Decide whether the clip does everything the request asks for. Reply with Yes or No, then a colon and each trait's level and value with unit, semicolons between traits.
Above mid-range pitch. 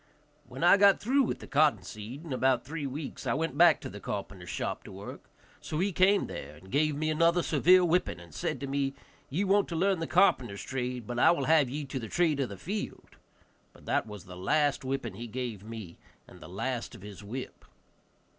No: medium, 140 Hz